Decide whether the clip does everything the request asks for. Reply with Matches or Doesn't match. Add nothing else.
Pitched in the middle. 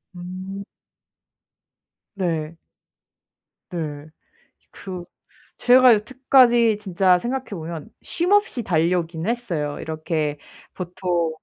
Matches